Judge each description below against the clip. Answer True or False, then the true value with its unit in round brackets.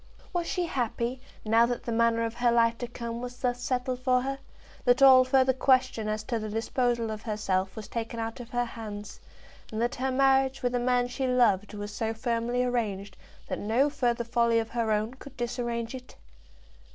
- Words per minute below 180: False (200 wpm)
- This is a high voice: True (240 Hz)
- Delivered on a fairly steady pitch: True (2.0 semitones)